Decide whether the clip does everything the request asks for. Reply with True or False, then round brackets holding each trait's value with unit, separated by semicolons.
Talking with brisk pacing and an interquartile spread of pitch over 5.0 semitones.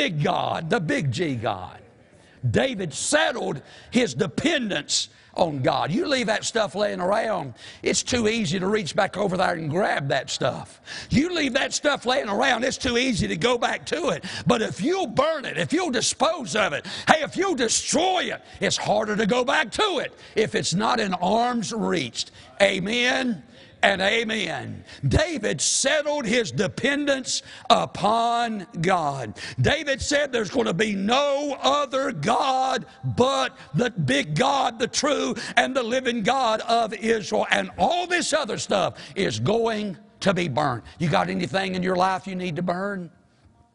False (165 wpm; 5.5 semitones)